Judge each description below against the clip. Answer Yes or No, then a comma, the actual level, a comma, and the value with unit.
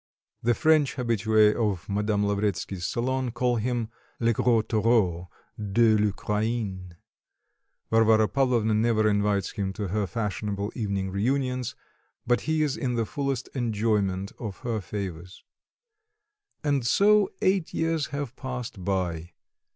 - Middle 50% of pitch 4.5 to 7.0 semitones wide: No, average, 3.6 semitones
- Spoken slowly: Yes, slow, 125 wpm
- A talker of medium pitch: No, low, 110 Hz